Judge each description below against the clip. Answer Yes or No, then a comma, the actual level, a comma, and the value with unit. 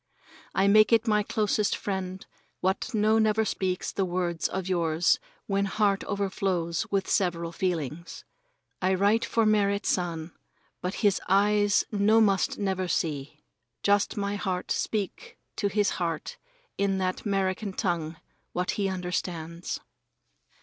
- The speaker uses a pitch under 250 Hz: Yes, high, 190 Hz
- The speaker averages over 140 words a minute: No, slow, 135 wpm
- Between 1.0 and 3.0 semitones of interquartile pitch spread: Yes, narrow, 2.5 semitones